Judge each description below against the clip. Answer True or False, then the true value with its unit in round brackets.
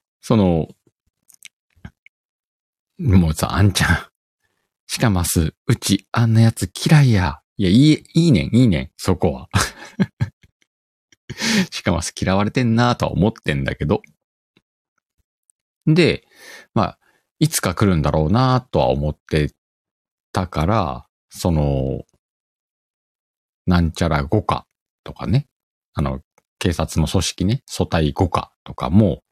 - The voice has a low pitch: True (95 Hz)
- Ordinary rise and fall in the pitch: False (7.7 semitones)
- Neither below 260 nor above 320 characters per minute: False (215 characters per minute)